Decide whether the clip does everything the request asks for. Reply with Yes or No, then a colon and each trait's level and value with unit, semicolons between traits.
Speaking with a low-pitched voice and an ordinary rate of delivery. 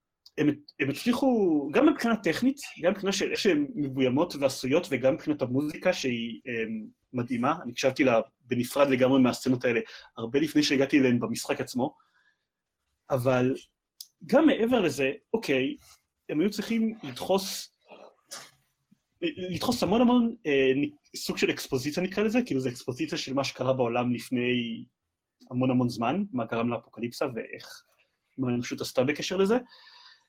No: medium, 145 Hz; average, 140 wpm